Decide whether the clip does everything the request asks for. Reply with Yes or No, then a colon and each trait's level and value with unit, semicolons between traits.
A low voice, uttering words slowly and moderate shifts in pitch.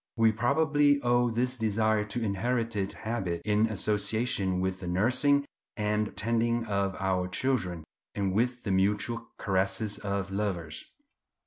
Yes: low, 105 Hz; slow, 130 wpm; average, 3.4 semitones